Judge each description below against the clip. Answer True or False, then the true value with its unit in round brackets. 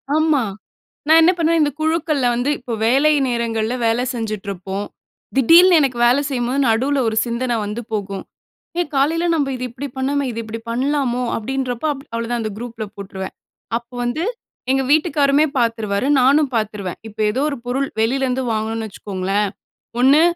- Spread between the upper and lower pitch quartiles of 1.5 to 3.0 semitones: False (4.1 semitones)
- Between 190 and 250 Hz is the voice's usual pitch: True (245 Hz)